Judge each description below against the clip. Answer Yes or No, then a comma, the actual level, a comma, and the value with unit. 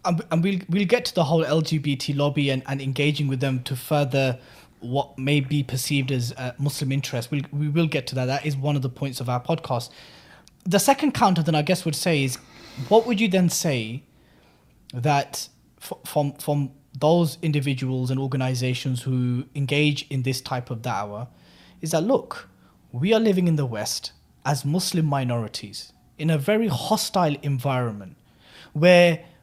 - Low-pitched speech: No, medium, 145 Hz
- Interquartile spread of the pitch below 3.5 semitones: No, average, 3.8 semitones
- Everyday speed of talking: Yes, average, 175 wpm